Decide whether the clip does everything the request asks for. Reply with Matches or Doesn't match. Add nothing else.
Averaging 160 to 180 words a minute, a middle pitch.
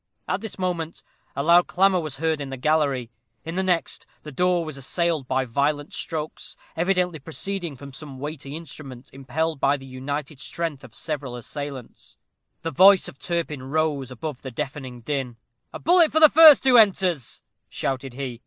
Matches